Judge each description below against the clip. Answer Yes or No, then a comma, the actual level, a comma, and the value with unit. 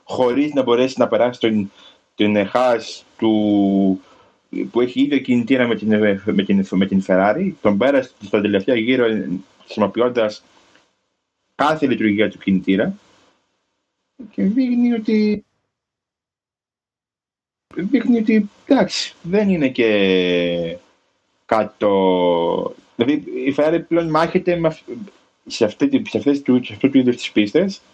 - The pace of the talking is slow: Yes, slow, 110 wpm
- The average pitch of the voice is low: Yes, low, 125 Hz